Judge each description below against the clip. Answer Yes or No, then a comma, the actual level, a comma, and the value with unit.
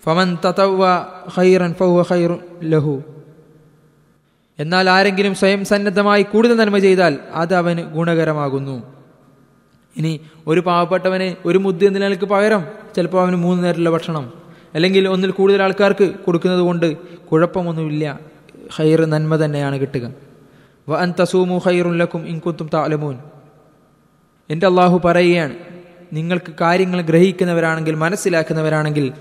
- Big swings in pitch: No, average, 2.9 semitones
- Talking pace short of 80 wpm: No, average, 85 wpm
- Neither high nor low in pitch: Yes, medium, 175 Hz